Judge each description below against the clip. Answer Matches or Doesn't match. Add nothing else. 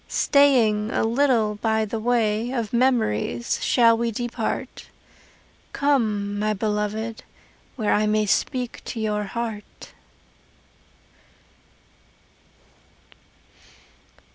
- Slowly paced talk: Matches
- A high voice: Matches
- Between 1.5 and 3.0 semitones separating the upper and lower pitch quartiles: Matches